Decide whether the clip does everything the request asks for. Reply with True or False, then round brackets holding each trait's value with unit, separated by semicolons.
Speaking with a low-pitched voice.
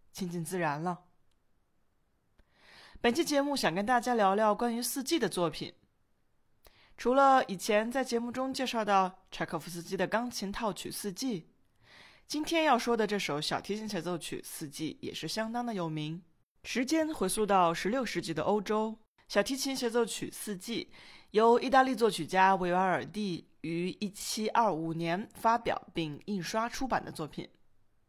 False (200 Hz)